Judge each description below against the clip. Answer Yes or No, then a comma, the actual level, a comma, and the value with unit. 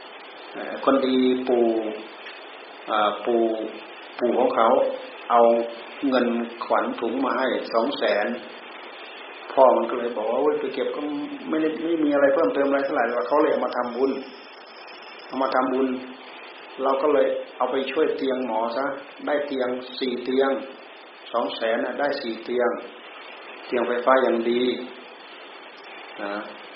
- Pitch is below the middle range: Yes, low, 130 Hz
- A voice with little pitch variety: No, average, 3.8 semitones